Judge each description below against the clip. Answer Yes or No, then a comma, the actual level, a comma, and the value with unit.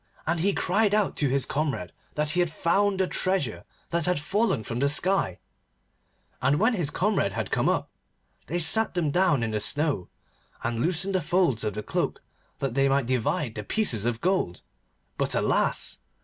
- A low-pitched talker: No, medium, 150 Hz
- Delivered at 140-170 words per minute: No, average, 185 wpm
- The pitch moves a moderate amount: No, wide, 7.0 semitones